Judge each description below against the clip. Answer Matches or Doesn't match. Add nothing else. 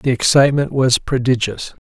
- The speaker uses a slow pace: Matches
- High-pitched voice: Doesn't match